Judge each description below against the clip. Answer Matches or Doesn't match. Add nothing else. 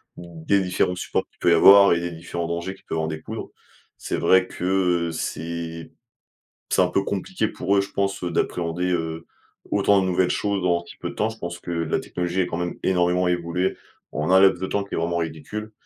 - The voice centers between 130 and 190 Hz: Doesn't match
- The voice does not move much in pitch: Matches